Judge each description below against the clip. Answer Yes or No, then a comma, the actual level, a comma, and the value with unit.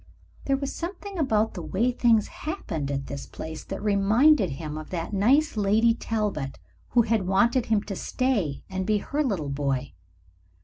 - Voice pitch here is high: Yes, high, 210 Hz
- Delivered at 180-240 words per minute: No, average, 170 wpm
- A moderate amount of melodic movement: No, wide, 6.7 semitones